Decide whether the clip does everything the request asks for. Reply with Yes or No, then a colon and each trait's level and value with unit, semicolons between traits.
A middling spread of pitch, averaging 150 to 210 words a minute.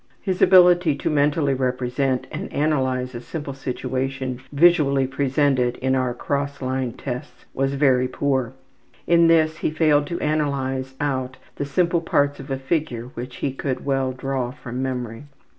No: narrow, 2.3 semitones; average, 155 wpm